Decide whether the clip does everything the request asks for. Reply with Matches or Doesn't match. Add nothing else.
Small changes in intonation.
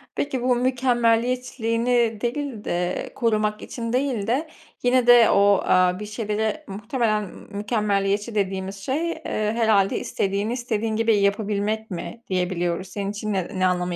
Doesn't match